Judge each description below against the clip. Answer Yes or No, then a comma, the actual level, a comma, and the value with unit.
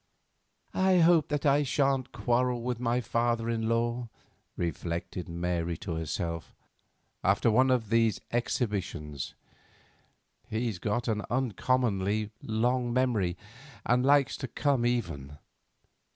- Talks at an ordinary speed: No, slow, 125 wpm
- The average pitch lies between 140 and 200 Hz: No, low, 115 Hz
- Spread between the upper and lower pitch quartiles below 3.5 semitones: No, average, 4.8 semitones